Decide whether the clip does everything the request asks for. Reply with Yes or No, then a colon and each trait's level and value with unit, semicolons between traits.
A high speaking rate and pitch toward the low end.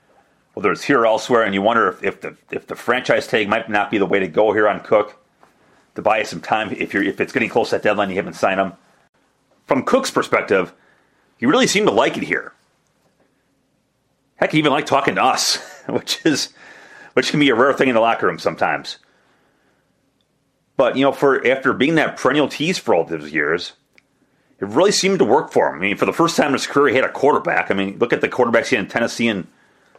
Yes: fast, 235 wpm; low, 110 Hz